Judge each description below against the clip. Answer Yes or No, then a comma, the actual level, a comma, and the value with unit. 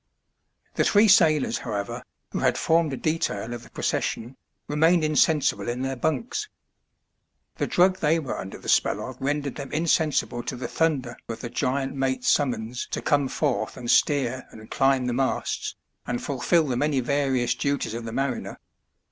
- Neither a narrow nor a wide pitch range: Yes, average, 3.8 semitones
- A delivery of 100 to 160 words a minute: No, average, 170 wpm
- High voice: No, low, 135 Hz